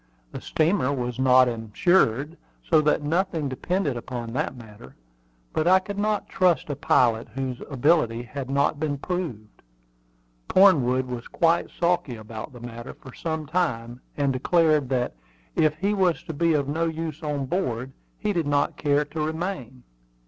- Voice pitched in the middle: Yes, medium, 145 Hz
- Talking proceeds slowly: No, average, 160 wpm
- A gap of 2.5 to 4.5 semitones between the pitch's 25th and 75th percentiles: No, average, 5.0 semitones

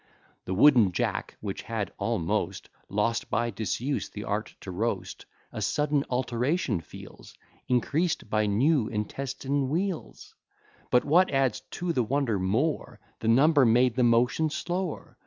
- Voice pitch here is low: Yes, low, 125 Hz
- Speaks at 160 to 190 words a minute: No, average, 140 wpm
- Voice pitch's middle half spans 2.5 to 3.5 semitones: No, average, 5.3 semitones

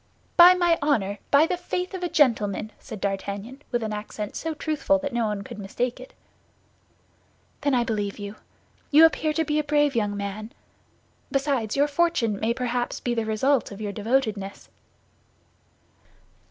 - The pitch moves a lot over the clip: Yes, wide, 5.8 semitones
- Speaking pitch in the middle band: No, high, 240 Hz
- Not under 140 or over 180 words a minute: Yes, average, 165 wpm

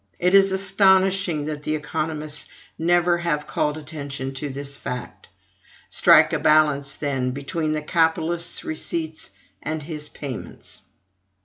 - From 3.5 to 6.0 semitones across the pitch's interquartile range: No, average, 2.9 semitones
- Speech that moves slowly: Yes, slow, 125 wpm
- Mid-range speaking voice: Yes, medium, 155 Hz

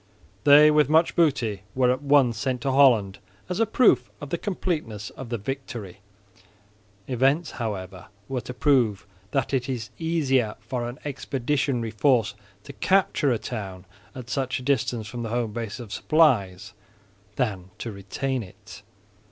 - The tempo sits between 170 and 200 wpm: No, average, 155 wpm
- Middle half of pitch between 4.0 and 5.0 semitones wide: Yes, average, 4.4 semitones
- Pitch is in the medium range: No, low, 125 Hz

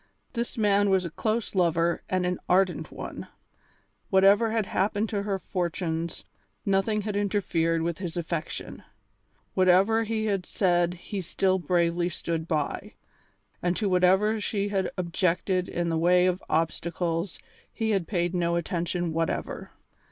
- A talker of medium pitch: Yes, medium, 180 Hz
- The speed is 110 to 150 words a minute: Yes, average, 145 wpm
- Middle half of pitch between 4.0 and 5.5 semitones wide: No, average, 2.8 semitones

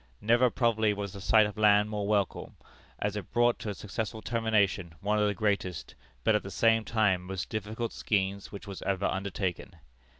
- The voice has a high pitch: No, low, 105 Hz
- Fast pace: No, average, 190 wpm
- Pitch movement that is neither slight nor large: No, narrow, 2.0 semitones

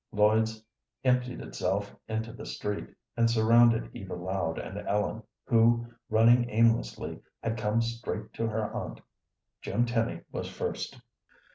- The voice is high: No, low, 110 Hz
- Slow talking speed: Yes, slow, 130 wpm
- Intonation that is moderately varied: No, narrow, 1.8 semitones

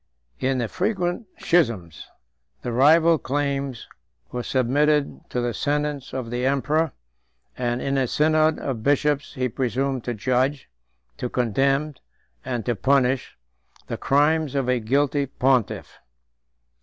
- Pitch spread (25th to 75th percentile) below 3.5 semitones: Yes, average, 2.9 semitones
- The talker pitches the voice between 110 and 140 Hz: Yes, low, 135 Hz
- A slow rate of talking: Yes, slow, 130 wpm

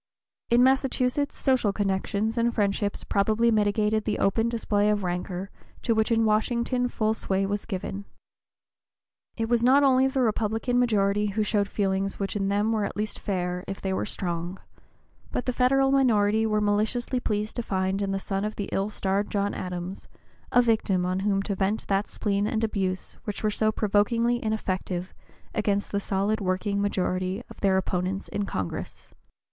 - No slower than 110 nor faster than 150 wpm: No, average, 175 wpm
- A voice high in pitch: Yes, high, 205 Hz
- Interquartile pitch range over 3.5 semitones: No, narrow, 2.5 semitones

